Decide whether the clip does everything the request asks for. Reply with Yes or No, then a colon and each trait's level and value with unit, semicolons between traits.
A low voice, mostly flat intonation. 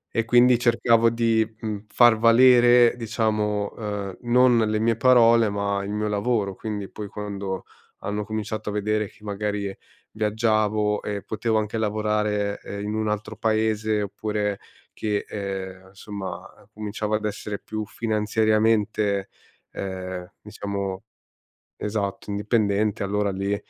Yes: low, 105 Hz; narrow, 1.5 semitones